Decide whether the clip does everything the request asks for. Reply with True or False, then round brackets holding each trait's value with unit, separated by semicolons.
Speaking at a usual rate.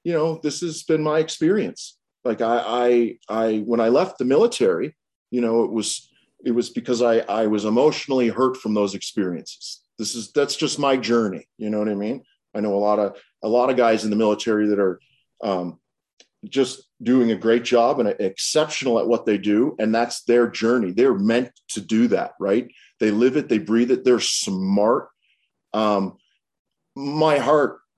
True (190 wpm)